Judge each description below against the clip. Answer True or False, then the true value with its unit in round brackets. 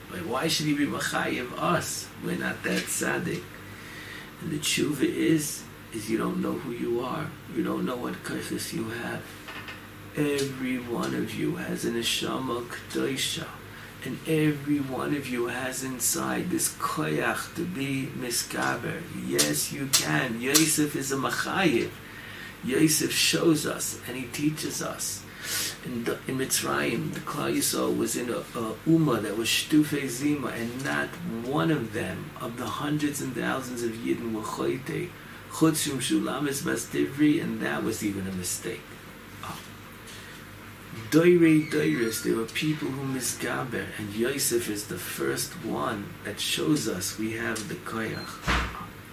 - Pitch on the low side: True (125 Hz)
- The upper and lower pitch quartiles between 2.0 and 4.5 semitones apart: False (5.4 semitones)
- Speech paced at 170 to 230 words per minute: False (155 wpm)